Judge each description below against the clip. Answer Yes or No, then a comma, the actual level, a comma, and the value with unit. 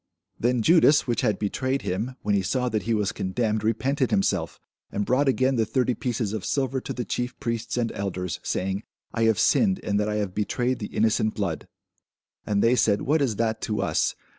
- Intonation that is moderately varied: Yes, average, 3.6 semitones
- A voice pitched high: No, low, 115 Hz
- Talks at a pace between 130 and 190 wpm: No, fast, 205 wpm